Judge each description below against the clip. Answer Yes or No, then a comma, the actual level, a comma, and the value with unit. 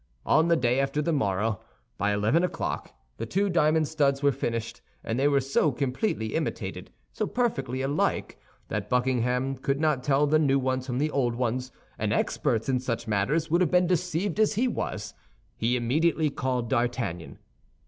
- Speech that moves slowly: No, average, 175 wpm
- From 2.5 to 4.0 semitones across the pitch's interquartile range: No, average, 4.4 semitones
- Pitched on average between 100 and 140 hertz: Yes, low, 135 Hz